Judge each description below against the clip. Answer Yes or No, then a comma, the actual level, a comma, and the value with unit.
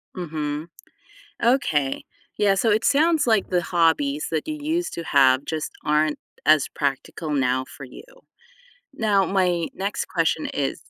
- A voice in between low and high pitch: Yes, medium, 165 Hz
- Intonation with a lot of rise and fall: Yes, wide, 5.8 semitones